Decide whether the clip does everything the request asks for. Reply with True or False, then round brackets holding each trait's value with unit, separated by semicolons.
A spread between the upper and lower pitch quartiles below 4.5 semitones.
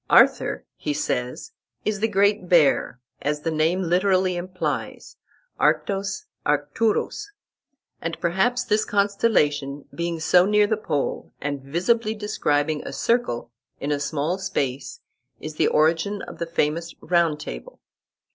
False (5.4 semitones)